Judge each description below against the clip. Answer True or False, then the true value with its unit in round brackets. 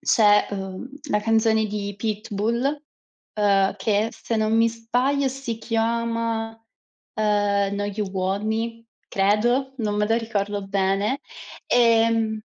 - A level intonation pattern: True (2.1 semitones)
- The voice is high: True (220 Hz)